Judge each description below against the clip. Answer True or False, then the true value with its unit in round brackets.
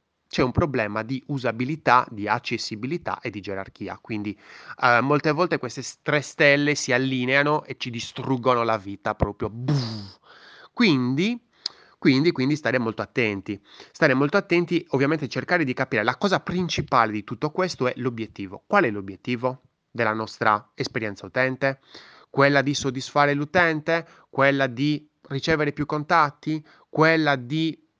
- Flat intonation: False (4.5 semitones)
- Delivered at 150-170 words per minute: False (135 wpm)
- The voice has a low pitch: True (130 Hz)